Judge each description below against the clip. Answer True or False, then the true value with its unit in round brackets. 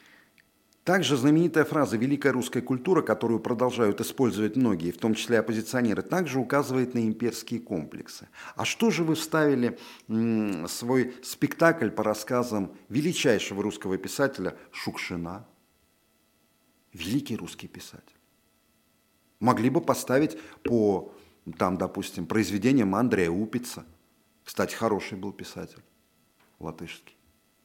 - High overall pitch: False (120 Hz)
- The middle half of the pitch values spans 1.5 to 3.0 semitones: False (4.2 semitones)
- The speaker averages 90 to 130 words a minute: True (110 wpm)